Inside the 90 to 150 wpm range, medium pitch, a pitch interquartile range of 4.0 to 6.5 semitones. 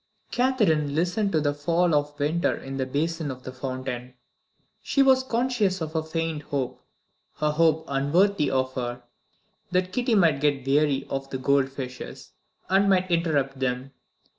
No: average, 160 wpm; medium, 150 Hz; average, 4.7 semitones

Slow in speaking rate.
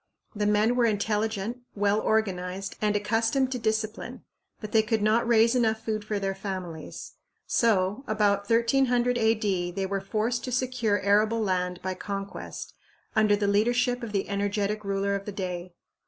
No: average, 160 wpm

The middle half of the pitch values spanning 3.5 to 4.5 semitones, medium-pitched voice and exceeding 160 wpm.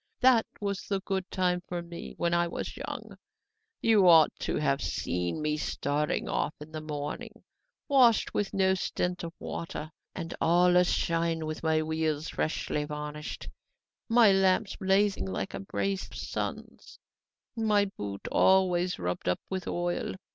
No: average, 3.8 semitones; medium, 175 Hz; average, 155 wpm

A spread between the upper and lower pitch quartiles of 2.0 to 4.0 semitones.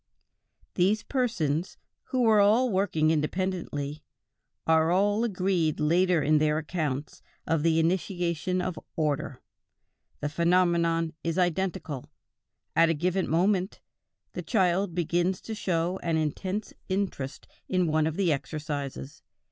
Yes: average, 3.3 semitones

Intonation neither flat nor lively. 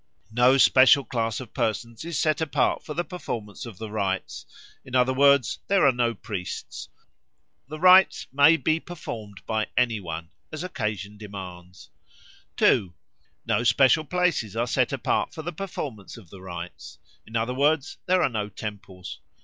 No: wide, 5.9 semitones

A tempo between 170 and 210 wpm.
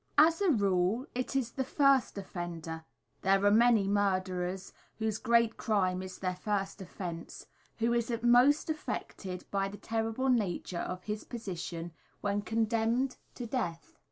No: average, 145 wpm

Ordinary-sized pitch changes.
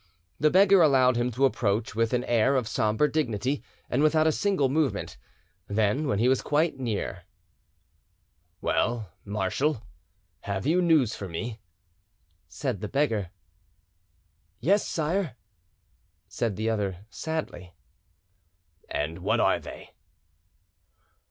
No: wide, 6.3 semitones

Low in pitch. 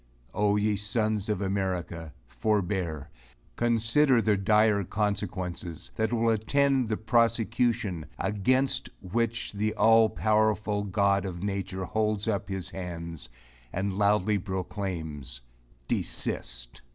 Yes: low, 105 Hz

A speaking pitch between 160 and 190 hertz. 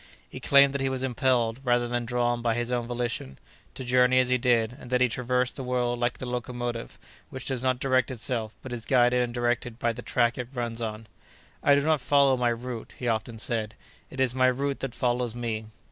No: low, 125 Hz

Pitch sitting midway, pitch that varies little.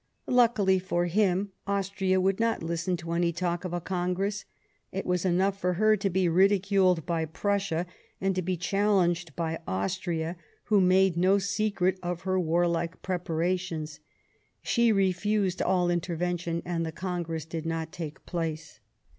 Yes: medium, 180 Hz; narrow, 2.3 semitones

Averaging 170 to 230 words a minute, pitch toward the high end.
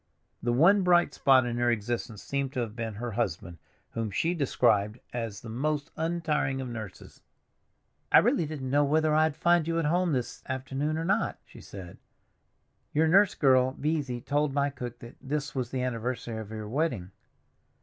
No: average, 180 wpm; low, 130 Hz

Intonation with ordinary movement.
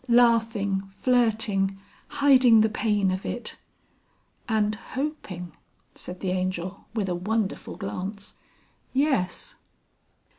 Yes: average, 3.6 semitones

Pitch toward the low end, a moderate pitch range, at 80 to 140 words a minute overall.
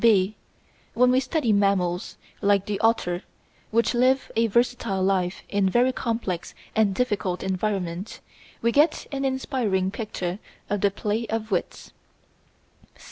No: high, 210 Hz; average, 3.9 semitones; slow, 135 wpm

